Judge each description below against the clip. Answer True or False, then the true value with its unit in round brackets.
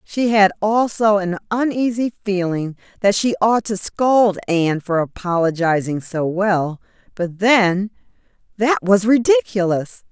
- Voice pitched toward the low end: False (200 Hz)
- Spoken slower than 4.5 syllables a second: True (4.0 syllables/s)